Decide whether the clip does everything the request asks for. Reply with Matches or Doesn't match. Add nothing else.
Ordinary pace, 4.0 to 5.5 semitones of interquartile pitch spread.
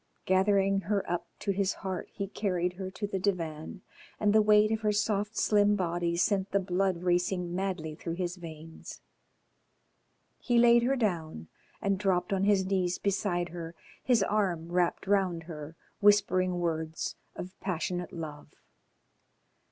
Doesn't match